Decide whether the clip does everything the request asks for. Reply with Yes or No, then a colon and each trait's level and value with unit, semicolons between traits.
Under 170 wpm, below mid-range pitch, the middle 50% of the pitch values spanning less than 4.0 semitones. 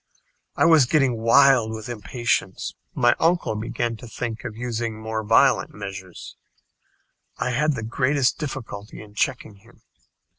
Yes: average, 140 wpm; low, 115 Hz; average, 2.8 semitones